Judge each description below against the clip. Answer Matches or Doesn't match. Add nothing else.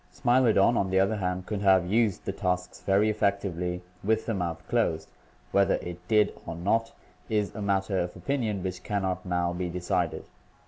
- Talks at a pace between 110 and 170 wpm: Doesn't match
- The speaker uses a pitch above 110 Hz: Doesn't match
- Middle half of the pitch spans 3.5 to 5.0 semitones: Doesn't match